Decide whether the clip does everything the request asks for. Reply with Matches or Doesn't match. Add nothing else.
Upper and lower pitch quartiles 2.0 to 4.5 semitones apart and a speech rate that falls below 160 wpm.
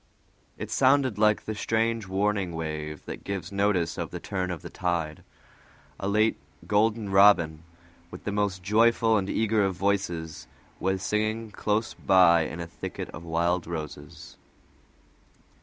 Matches